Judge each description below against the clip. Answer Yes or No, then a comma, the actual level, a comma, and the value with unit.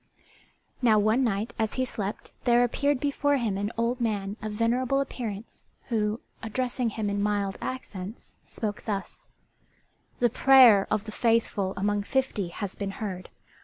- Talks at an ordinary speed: Yes, average, 155 wpm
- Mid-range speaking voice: No, high, 220 Hz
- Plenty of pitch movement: No, average, 3.2 semitones